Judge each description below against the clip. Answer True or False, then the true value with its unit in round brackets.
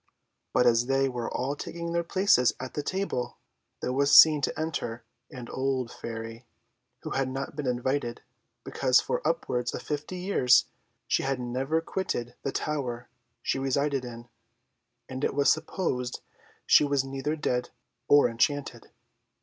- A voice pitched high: False (135 Hz)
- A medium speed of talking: True (150 wpm)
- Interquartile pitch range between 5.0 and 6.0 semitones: False (2.9 semitones)